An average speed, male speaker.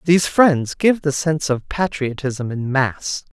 Yes: average, 160 wpm; male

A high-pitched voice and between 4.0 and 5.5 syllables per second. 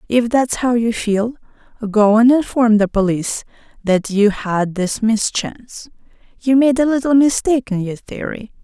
Yes: high, 230 Hz; 4.6 syllables/s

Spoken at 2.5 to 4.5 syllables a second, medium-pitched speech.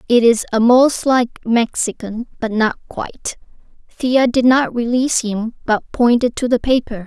No: 4.4 syllables/s; high, 240 Hz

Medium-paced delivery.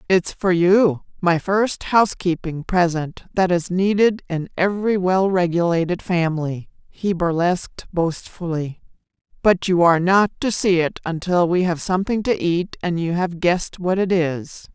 Yes: average, 155 wpm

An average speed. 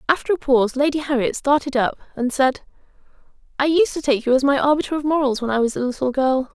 No: fast, 220 wpm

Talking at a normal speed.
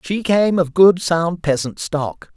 Yes: average, 180 wpm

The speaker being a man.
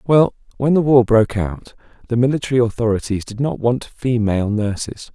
Yes: male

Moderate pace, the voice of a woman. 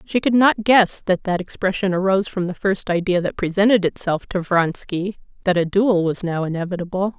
Yes: average, 185 wpm; female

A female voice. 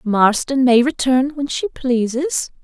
Yes: female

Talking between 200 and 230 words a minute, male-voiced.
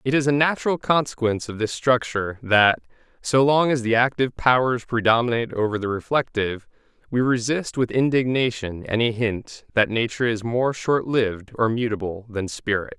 No: average, 155 wpm; male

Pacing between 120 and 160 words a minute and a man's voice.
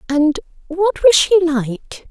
No: average, 140 wpm; female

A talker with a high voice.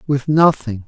No: medium, 140 Hz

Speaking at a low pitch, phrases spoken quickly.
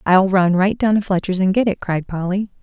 No: high, 190 Hz; fast, 250 wpm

